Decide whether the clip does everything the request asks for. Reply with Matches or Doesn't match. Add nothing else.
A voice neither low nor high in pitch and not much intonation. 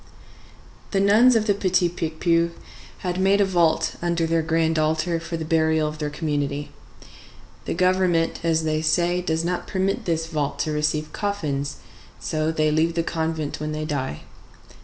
Matches